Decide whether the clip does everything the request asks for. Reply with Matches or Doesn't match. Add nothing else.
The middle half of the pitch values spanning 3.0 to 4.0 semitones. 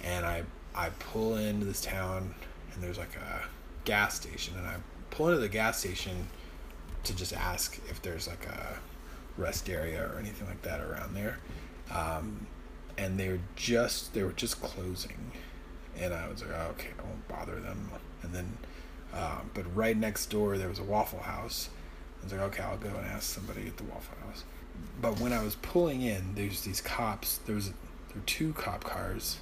Matches